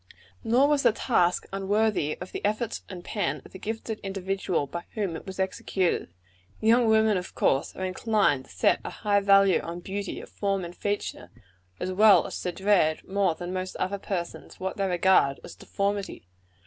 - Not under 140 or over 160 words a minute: No, average, 180 wpm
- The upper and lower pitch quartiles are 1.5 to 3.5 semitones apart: Yes, narrow, 2.4 semitones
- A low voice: No, high, 195 Hz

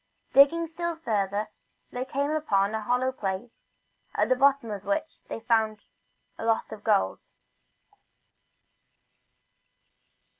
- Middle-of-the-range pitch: No, high, 240 Hz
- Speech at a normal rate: No, slow, 120 wpm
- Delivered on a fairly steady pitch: No, average, 4.9 semitones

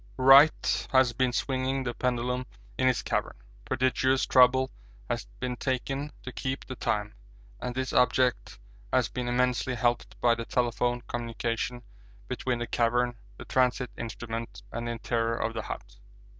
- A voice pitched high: No, low, 125 Hz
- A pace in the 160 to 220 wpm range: No, average, 150 wpm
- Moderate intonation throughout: No, narrow, 1.5 semitones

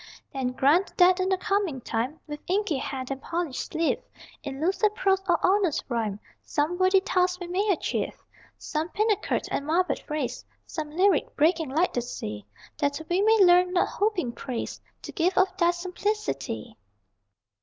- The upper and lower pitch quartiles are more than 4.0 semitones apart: Yes, average, 5.0 semitones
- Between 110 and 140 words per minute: No, average, 165 wpm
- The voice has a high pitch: Yes, very high, 345 Hz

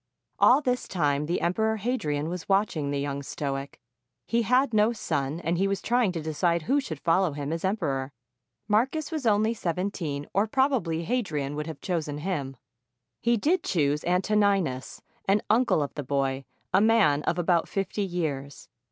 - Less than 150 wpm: No, average, 170 wpm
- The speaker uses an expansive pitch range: Yes, wide, 6.7 semitones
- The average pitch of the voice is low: No, medium, 175 Hz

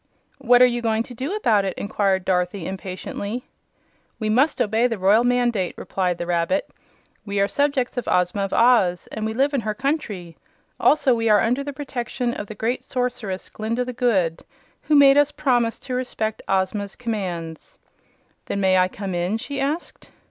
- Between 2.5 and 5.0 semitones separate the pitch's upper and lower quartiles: Yes, average, 4.6 semitones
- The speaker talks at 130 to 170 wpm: No, average, 180 wpm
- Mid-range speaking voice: No, high, 225 Hz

